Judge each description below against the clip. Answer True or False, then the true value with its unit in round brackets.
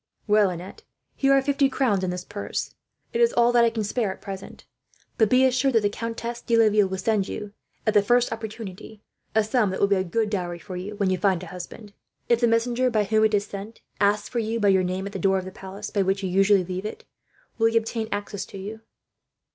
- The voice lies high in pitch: True (210 Hz)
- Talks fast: True (240 wpm)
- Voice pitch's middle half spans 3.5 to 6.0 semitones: False (3.0 semitones)